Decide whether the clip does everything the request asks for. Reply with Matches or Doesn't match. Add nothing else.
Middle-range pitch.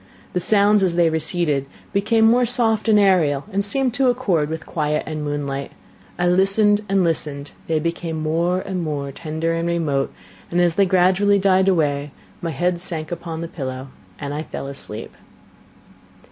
Matches